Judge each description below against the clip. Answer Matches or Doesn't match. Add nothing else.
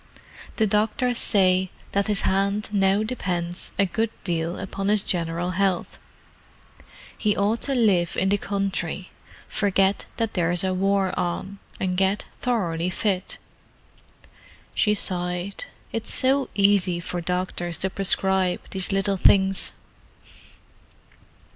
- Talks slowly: Matches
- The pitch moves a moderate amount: Doesn't match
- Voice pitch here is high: Matches